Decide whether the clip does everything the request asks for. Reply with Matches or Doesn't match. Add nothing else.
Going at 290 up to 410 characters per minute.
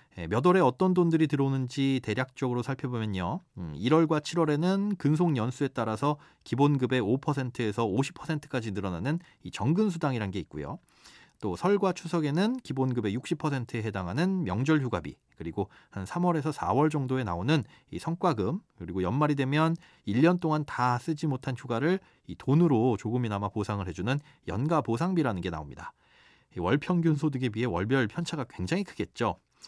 Matches